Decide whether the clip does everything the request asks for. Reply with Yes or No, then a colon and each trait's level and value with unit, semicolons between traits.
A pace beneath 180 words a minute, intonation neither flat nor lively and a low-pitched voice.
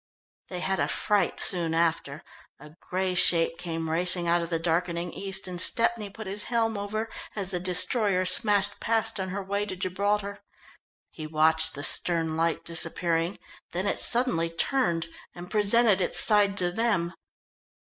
No: average, 160 wpm; average, 3.3 semitones; medium, 185 Hz